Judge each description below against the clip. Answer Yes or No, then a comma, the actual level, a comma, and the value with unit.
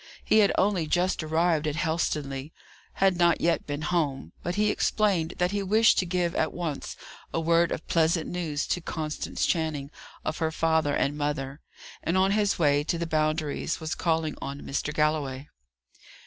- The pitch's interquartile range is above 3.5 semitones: No, narrow, 2.6 semitones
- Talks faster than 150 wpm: Yes, average, 175 wpm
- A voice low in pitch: No, medium, 160 Hz